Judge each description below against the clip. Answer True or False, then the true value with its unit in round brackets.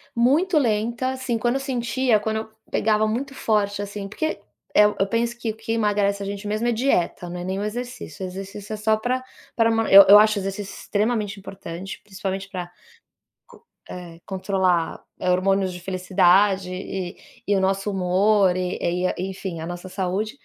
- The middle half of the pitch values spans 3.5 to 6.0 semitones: False (2.9 semitones)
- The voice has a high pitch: True (205 Hz)